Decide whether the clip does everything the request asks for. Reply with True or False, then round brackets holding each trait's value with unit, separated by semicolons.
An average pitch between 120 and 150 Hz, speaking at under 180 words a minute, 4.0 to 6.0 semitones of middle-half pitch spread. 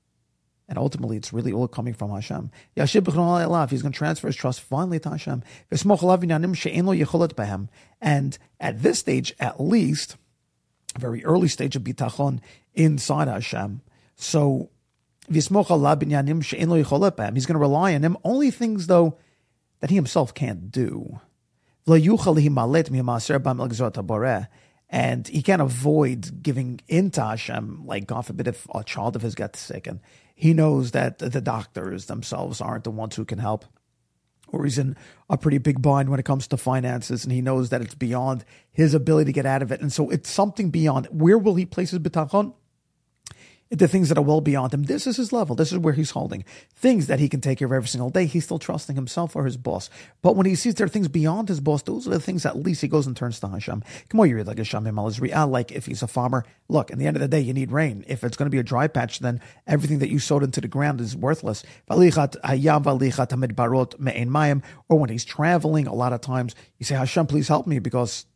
False (140 Hz; 195 wpm; 4.4 semitones)